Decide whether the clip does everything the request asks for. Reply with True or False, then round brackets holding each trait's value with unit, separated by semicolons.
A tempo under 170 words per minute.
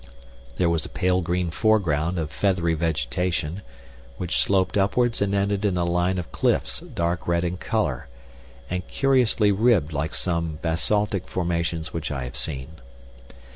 True (150 wpm)